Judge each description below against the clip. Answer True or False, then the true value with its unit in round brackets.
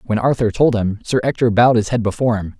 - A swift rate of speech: True (255 wpm)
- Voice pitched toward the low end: True (115 Hz)